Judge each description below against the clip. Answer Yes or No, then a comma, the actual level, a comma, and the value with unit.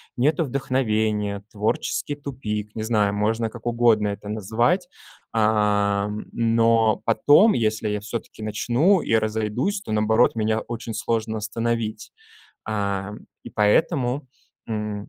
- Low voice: Yes, low, 110 Hz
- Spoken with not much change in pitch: Yes, narrow, 2.0 semitones